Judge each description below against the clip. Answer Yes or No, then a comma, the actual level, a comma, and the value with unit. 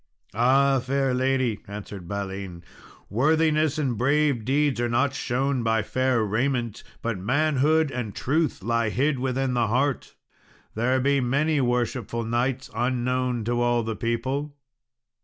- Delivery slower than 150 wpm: Yes, slow, 135 wpm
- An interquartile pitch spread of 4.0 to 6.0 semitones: No, average, 2.9 semitones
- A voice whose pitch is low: Yes, low, 125 Hz